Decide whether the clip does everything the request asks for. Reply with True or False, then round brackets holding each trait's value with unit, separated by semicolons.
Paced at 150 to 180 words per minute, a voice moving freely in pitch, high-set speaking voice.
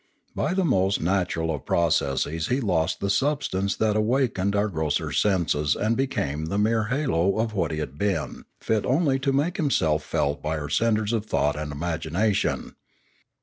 False (170 wpm; 6.4 semitones; 100 Hz)